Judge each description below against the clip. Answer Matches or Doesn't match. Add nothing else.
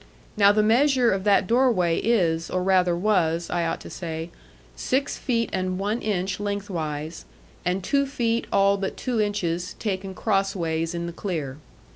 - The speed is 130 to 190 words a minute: Matches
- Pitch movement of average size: Matches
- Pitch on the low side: Doesn't match